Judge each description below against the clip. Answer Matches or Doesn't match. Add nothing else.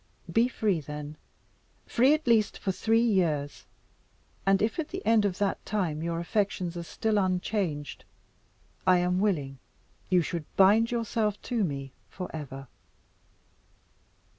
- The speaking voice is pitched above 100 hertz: Matches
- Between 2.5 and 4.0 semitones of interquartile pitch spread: Doesn't match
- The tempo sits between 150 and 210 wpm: Doesn't match